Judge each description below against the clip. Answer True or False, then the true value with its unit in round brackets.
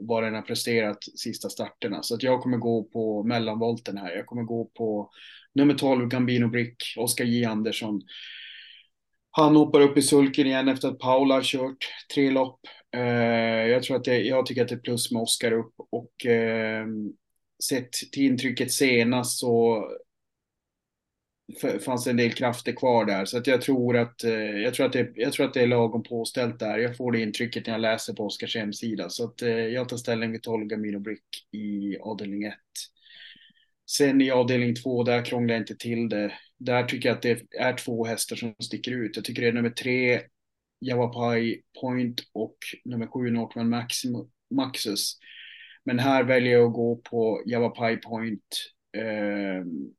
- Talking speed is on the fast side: False (175 wpm)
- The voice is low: True (120 Hz)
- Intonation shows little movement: True (1.9 semitones)